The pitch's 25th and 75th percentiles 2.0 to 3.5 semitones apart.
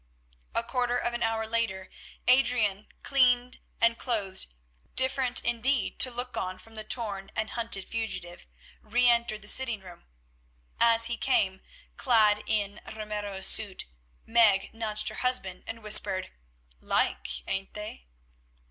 Yes: average, 2.9 semitones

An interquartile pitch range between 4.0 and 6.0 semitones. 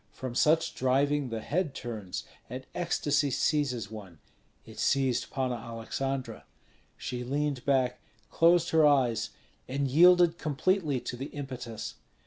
No: average, 3.3 semitones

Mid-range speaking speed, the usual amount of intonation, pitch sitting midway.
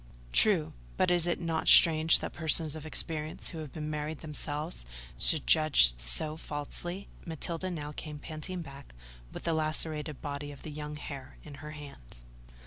No: average, 165 wpm; narrow, 1.8 semitones; medium, 155 Hz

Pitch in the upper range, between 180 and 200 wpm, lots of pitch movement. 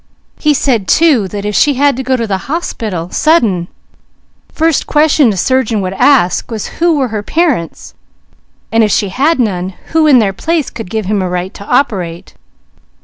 Yes: high, 230 Hz; average, 185 wpm; wide, 7.0 semitones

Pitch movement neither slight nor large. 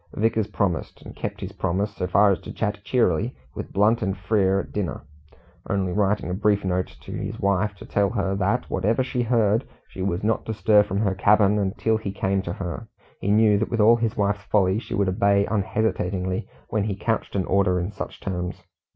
No: narrow, 2.2 semitones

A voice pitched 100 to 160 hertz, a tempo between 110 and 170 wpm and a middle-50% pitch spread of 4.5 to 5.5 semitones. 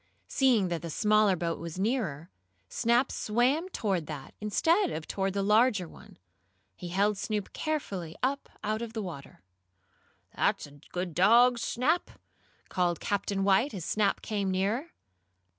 No: high, 205 Hz; average, 145 wpm; average, 4.9 semitones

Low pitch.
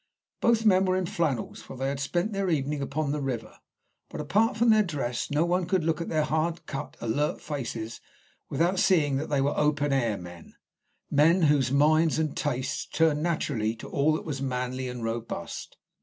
No: medium, 150 Hz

